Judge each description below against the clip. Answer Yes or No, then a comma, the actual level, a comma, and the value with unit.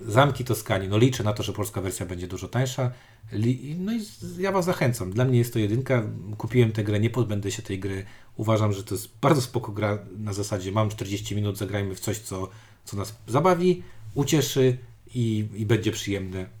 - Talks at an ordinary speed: No, fast, 195 wpm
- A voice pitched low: Yes, low, 110 Hz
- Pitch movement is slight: No, average, 3.4 semitones